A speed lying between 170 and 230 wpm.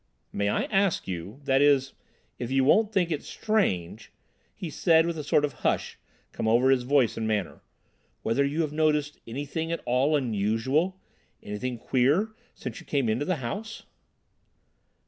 No: average, 155 wpm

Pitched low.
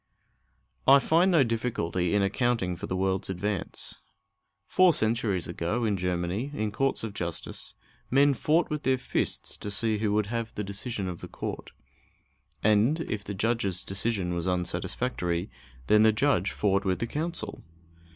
Yes: low, 105 Hz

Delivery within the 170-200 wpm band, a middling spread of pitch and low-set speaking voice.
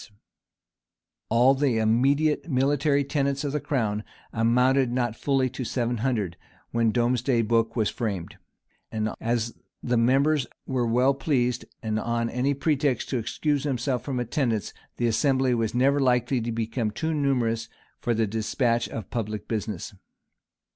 No: average, 145 wpm; average, 3.1 semitones; low, 120 Hz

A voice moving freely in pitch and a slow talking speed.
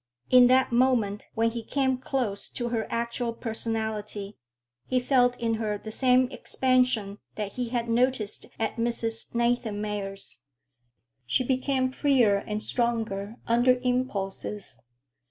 No: average, 3.0 semitones; slow, 125 wpm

